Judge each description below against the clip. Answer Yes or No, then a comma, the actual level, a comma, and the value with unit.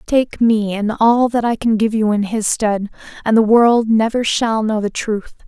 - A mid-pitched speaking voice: No, high, 220 Hz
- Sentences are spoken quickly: Yes, fast, 220 wpm